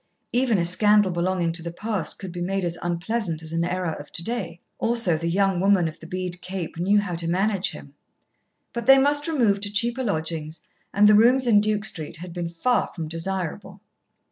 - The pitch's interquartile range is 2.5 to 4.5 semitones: Yes, average, 3.9 semitones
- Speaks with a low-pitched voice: No, medium, 185 Hz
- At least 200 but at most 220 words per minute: Yes, fast, 205 wpm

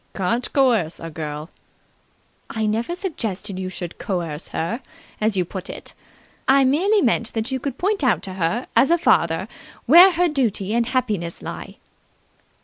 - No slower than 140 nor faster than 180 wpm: Yes, average, 165 wpm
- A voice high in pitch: Yes, high, 225 Hz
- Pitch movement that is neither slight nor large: No, wide, 6.7 semitones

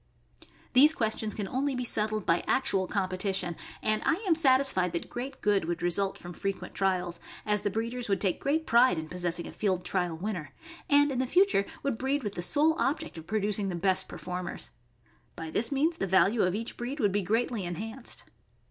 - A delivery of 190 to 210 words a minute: Yes, average, 200 wpm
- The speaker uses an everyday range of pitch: No, wide, 5.9 semitones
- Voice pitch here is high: Yes, high, 210 Hz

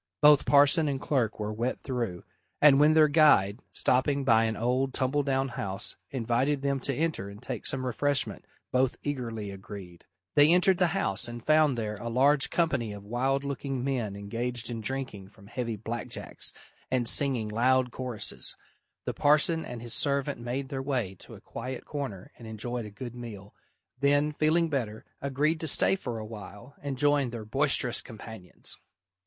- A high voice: No, low, 130 Hz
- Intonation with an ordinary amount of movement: Yes, average, 4.1 semitones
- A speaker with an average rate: Yes, average, 175 wpm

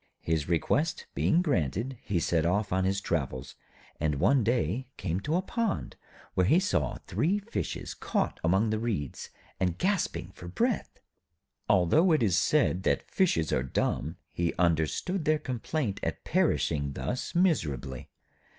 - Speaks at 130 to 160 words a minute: Yes, average, 150 wpm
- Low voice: Yes, very low, 95 Hz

